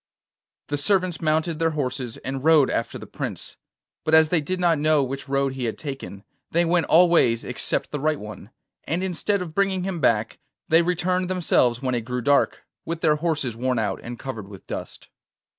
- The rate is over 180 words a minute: Yes, average, 195 wpm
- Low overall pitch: No, medium, 150 Hz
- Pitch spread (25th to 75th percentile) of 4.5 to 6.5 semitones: Yes, average, 5.0 semitones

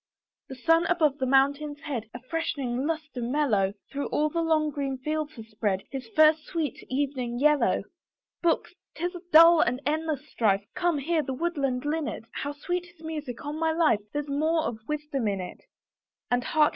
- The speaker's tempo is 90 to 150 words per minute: No, average, 180 wpm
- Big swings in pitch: No, average, 3.7 semitones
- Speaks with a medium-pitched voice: No, very high, 295 Hz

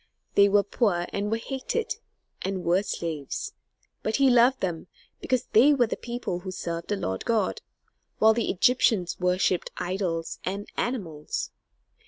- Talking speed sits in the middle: Yes, average, 150 wpm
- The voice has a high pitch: Yes, high, 200 Hz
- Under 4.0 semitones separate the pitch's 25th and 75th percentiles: No, average, 4.9 semitones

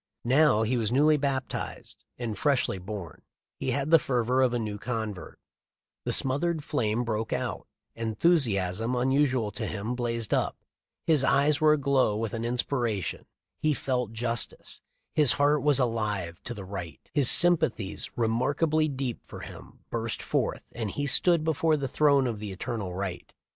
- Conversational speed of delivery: Yes, average, 160 wpm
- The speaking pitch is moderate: No, low, 125 Hz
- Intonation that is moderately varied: Yes, average, 4.5 semitones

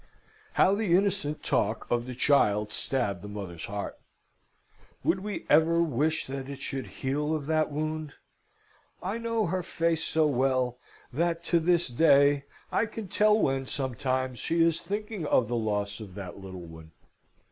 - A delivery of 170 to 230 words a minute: No, average, 160 wpm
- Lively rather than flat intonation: Yes, wide, 5.8 semitones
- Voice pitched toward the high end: No, medium, 145 Hz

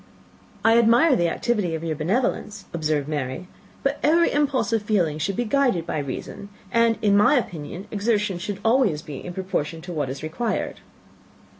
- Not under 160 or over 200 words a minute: Yes, average, 170 wpm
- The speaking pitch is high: Yes, high, 195 Hz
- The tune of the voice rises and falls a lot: Yes, wide, 6.6 semitones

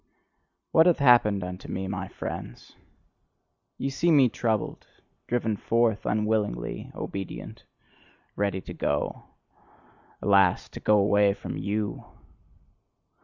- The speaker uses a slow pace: Yes, slow, 110 wpm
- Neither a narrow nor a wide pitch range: Yes, average, 3.2 semitones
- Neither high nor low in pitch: No, low, 105 Hz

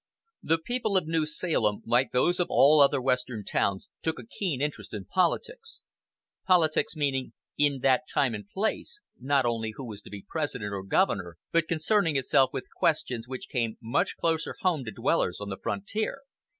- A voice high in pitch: No, medium, 140 Hz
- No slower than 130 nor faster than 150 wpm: No, average, 175 wpm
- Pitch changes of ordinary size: No, wide, 6.4 semitones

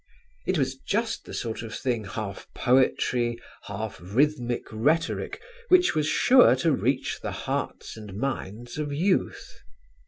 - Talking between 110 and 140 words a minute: Yes, slow, 135 wpm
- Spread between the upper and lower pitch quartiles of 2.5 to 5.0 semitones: No, wide, 5.6 semitones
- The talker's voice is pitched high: No, low, 125 Hz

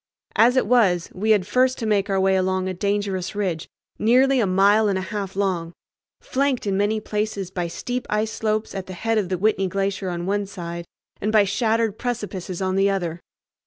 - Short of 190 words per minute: No, average, 200 wpm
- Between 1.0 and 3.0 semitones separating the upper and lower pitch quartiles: Yes, narrow, 2.6 semitones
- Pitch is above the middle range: Yes, high, 200 Hz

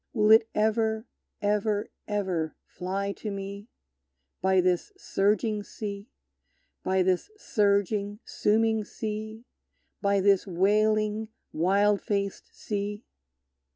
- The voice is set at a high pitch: Yes, high, 205 Hz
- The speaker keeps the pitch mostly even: Yes, narrow, 1.5 semitones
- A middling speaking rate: No, slow, 100 wpm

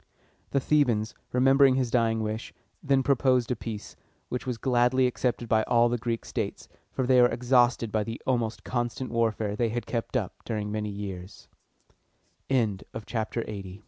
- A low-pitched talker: Yes, low, 120 Hz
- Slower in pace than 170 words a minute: Yes, average, 155 wpm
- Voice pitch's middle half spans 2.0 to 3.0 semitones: Yes, narrow, 2.5 semitones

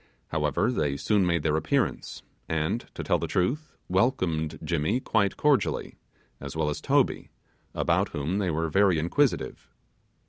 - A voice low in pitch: Yes, very low, 85 Hz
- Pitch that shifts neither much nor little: No, wide, 5.8 semitones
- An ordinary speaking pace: Yes, average, 145 wpm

